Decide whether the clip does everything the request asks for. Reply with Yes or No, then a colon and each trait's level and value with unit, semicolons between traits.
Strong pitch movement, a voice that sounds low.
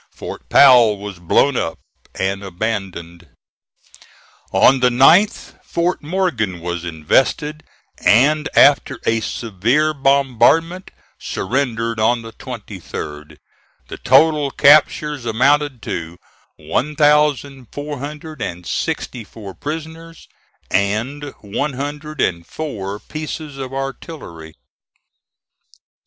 Yes: wide, 6.5 semitones; low, 130 Hz